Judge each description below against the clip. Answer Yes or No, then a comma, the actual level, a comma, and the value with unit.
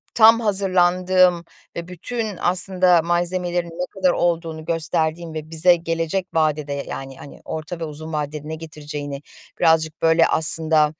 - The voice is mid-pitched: Yes, medium, 165 Hz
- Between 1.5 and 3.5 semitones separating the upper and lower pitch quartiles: Yes, narrow, 2.4 semitones